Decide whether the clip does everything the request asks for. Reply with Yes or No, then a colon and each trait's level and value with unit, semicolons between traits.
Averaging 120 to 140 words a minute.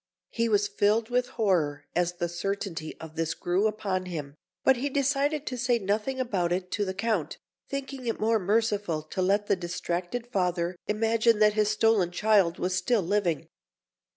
No: average, 175 wpm